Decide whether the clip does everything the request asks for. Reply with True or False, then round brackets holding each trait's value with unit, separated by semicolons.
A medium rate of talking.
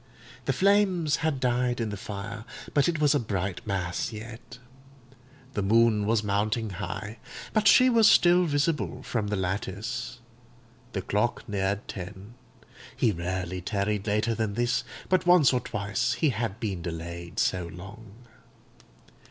True (145 wpm)